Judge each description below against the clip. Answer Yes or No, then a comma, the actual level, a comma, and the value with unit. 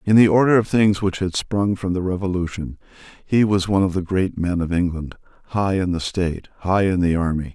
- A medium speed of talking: No, fast, 225 wpm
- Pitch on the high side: No, very low, 95 Hz